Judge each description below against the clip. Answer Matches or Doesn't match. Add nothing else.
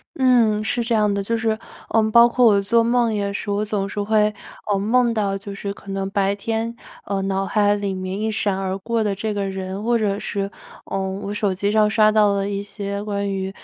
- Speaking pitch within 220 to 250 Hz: Doesn't match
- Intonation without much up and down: Matches